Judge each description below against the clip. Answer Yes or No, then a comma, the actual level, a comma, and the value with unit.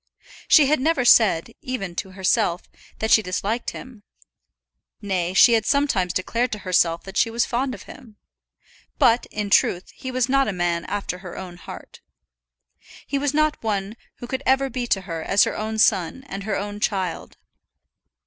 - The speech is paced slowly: No, average, 175 wpm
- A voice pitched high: Yes, high, 215 Hz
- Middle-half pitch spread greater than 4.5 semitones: Yes, average, 5.1 semitones